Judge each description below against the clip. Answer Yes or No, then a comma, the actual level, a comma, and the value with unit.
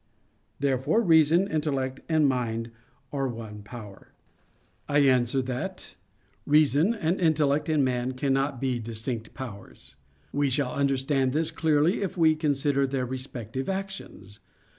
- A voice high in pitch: No, low, 135 Hz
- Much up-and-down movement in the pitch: No, average, 3.5 semitones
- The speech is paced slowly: Yes, slow, 125 wpm